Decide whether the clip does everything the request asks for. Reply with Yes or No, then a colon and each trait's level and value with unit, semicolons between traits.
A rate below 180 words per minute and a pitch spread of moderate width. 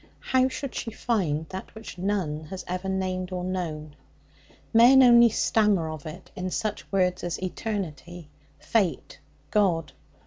Yes: average, 140 wpm; average, 4.1 semitones